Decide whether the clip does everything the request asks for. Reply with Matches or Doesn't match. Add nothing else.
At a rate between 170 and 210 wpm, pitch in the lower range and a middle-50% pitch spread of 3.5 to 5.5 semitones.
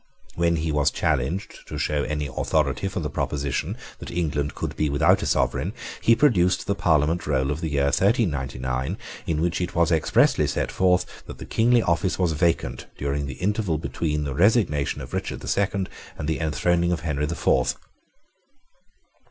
Matches